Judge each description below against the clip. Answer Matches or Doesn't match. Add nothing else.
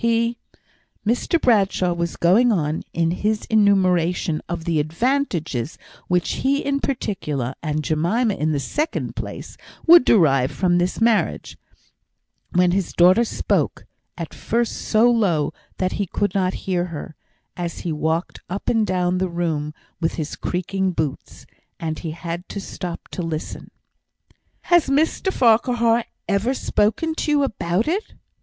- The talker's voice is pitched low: Doesn't match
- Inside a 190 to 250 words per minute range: Doesn't match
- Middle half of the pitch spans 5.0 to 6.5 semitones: Matches